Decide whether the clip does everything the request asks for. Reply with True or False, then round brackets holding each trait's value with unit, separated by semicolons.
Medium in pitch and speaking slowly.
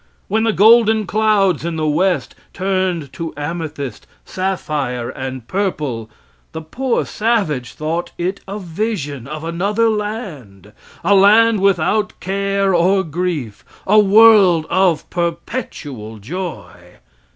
True (180 Hz; 120 wpm)